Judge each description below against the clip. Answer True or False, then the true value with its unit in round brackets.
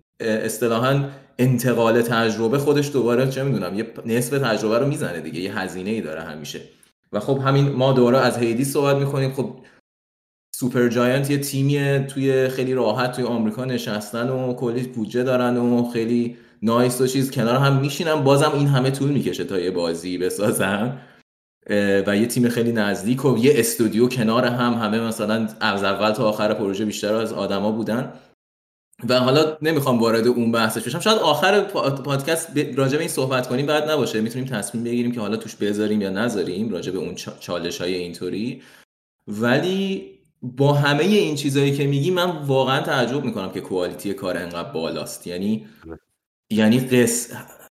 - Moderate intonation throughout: True (3.7 semitones)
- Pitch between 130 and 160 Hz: False (120 Hz)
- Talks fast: True (165 wpm)